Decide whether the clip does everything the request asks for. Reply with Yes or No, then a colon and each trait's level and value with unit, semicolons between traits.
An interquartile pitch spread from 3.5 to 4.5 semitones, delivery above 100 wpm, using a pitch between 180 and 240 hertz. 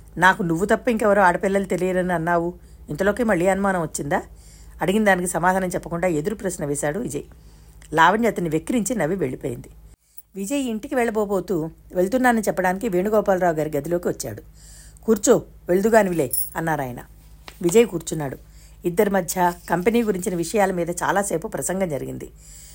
Yes: average, 3.8 semitones; fast, 125 wpm; medium, 185 Hz